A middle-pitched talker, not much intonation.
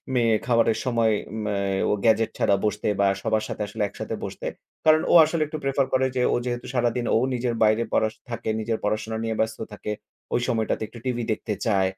No: low, 115 Hz; narrow, 2.1 semitones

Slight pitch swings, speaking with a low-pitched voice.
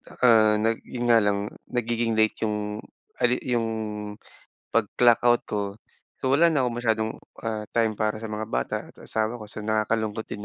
Yes: narrow, 1.8 semitones; low, 110 Hz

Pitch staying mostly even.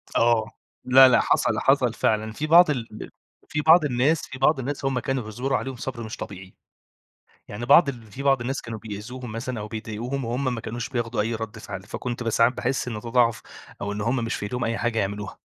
No: average, 3.2 semitones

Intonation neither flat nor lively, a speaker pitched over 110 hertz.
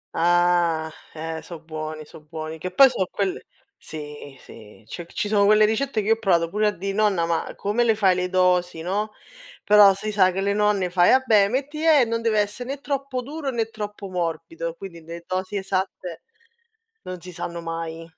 Yes: average, 4.3 semitones; medium, 185 Hz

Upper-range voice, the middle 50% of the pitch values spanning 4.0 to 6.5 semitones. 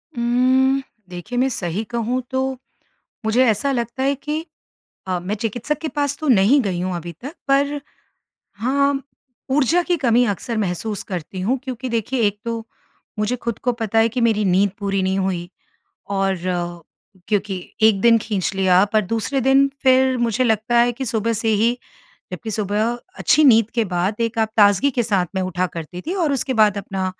Yes: high, 230 Hz; average, 4.6 semitones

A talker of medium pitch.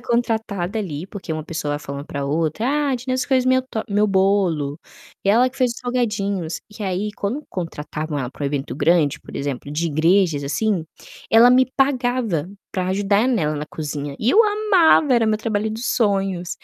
No: high, 200 Hz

